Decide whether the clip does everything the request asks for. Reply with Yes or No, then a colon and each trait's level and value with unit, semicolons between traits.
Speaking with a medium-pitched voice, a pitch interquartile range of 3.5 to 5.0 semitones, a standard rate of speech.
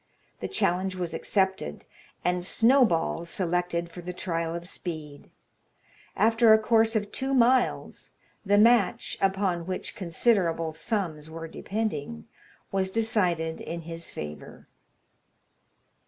No: medium, 180 Hz; average, 4.7 semitones; slow, 115 wpm